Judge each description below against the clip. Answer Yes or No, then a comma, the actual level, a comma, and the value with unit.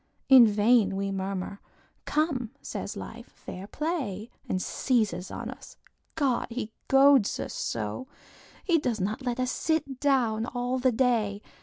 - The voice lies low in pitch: No, high, 240 Hz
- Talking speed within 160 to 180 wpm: No, average, 145 wpm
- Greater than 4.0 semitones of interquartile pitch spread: Yes, average, 4.8 semitones